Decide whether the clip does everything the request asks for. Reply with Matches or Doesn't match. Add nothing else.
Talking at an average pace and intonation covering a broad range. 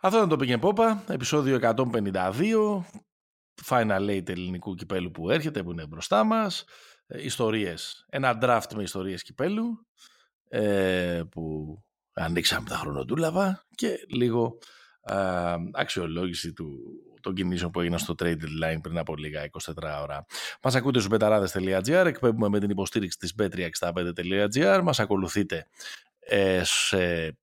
Matches